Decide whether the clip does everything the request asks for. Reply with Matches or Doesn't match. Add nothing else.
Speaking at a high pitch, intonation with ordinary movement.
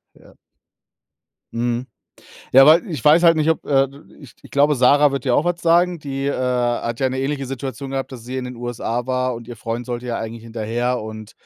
Doesn't match